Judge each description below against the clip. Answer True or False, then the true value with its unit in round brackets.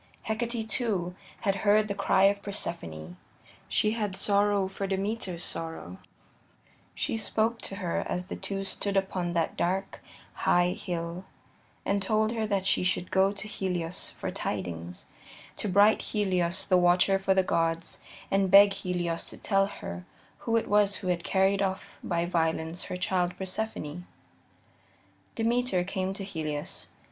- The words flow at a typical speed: True (150 wpm)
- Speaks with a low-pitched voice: False (190 Hz)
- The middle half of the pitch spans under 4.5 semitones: True (2.5 semitones)